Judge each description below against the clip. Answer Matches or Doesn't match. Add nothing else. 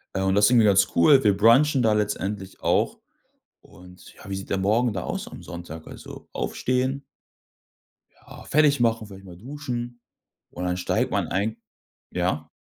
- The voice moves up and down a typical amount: Matches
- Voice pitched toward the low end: Matches